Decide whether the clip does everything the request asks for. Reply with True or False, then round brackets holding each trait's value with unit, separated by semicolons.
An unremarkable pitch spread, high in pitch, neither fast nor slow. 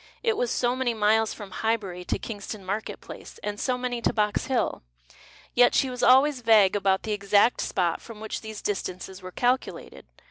True (3.6 semitones; 220 Hz; 185 wpm)